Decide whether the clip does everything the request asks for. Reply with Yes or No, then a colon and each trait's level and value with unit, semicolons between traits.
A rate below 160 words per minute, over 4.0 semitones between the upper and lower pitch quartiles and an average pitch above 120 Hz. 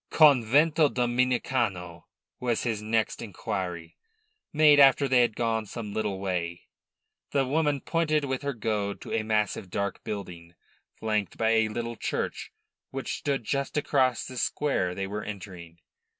No: average, 145 wpm; average, 5.1 semitones; low, 115 Hz